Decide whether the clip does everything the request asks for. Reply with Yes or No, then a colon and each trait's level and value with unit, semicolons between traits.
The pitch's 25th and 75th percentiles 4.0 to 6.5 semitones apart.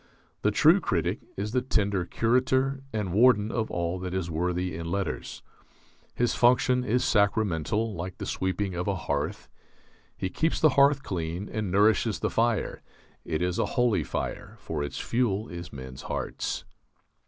Yes: average, 5.1 semitones